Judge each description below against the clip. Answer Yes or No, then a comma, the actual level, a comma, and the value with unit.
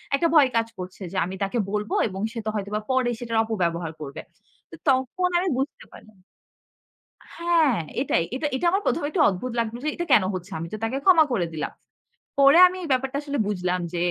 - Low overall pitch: No, high, 230 Hz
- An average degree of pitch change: No, wide, 6.9 semitones